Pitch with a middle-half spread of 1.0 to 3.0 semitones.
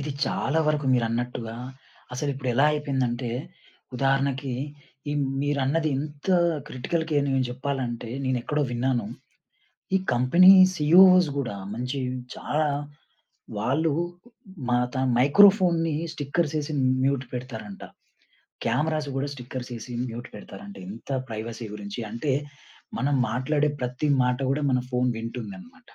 No: average, 3.4 semitones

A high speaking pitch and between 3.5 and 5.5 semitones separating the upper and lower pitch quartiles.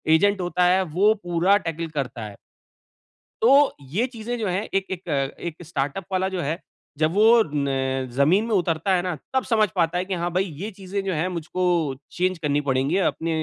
No: medium, 180 Hz; average, 3.8 semitones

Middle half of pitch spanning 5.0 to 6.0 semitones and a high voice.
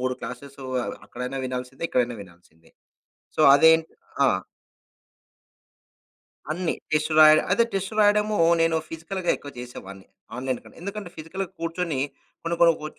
No: wide, 5.5 semitones; medium, 155 Hz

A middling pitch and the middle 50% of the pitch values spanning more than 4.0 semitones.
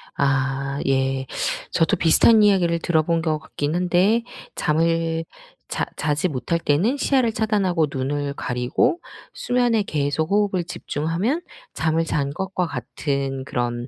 Yes: medium, 165 Hz; average, 5.2 semitones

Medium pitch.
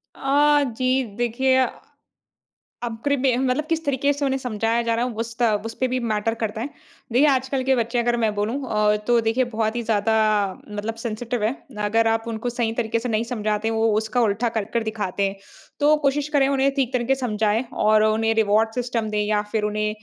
No: high, 230 Hz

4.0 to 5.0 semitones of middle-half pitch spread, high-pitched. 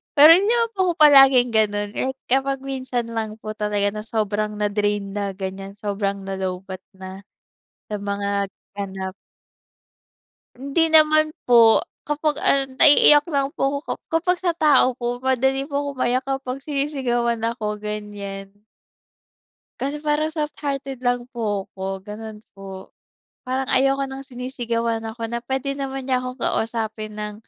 Yes: average, 4.7 semitones; high, 240 Hz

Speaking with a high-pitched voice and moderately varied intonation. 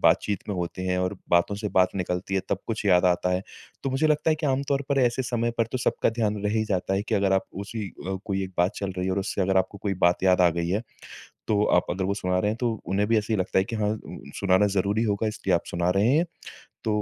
No: low, 100 Hz; average, 3.1 semitones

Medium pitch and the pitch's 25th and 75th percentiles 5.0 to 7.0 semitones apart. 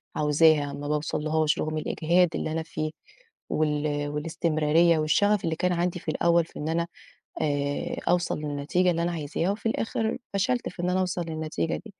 No: medium, 160 Hz; average, 2.7 semitones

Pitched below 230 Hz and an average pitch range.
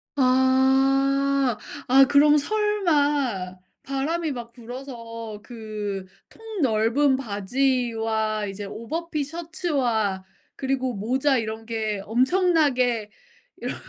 No: very high, 260 Hz; average, 4.3 semitones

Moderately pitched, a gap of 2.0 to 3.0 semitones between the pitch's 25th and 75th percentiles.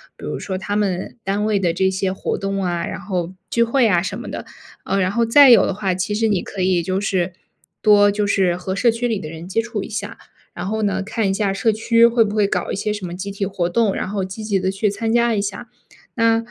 No: high, 200 Hz; narrow, 2.6 semitones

